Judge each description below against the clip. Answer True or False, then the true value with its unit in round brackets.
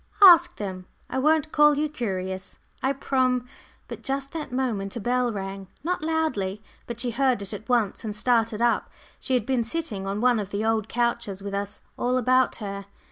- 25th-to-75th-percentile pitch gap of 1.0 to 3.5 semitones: False (4.7 semitones)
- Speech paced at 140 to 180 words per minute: False (195 wpm)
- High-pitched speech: True (235 Hz)